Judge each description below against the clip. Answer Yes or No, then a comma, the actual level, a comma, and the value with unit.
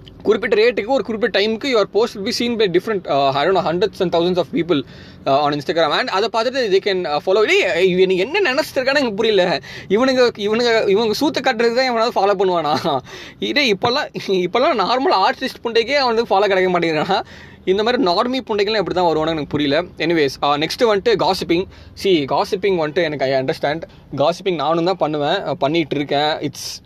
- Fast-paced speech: Yes, fast, 170 wpm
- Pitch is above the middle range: Yes, high, 195 Hz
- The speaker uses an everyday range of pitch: No, wide, 6.3 semitones